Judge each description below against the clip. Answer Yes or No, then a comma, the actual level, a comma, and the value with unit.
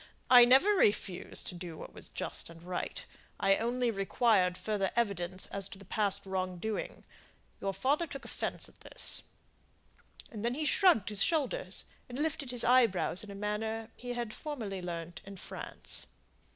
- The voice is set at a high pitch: Yes, high, 210 Hz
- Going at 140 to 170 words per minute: Yes, average, 165 wpm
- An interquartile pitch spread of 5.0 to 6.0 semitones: No, average, 4.4 semitones